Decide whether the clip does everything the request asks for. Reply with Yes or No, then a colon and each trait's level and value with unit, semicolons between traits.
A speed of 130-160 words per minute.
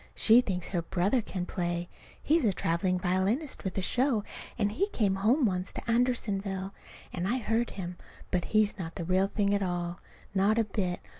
No: average, 190 wpm